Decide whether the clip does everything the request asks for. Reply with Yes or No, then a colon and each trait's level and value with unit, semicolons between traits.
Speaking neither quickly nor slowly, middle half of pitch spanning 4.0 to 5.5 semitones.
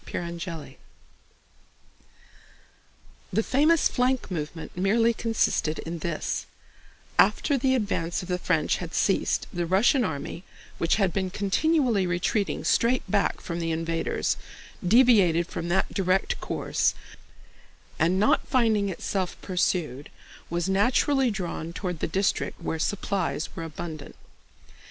No: slow, 125 wpm; average, 4.7 semitones